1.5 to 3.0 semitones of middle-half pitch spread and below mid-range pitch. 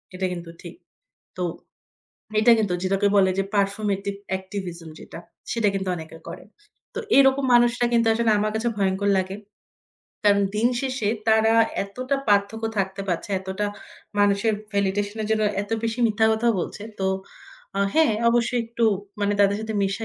No: narrow, 2.5 semitones; high, 205 Hz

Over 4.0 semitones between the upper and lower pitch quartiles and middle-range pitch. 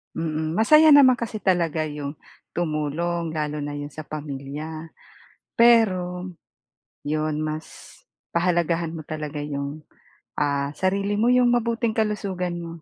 Yes: average, 4.8 semitones; medium, 165 Hz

